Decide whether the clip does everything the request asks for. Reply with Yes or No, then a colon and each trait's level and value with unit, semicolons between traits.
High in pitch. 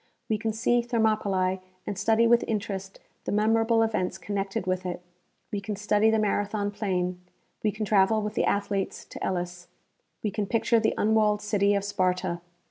Yes: high, 205 Hz